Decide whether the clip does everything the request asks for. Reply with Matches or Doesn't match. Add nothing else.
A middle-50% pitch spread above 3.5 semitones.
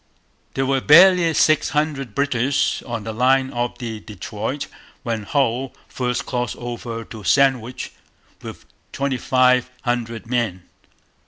Doesn't match